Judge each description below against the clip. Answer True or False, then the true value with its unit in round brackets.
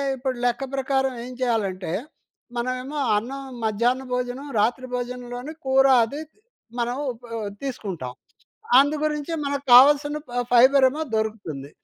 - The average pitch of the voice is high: True (255 Hz)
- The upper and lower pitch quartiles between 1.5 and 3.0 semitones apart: True (2.6 semitones)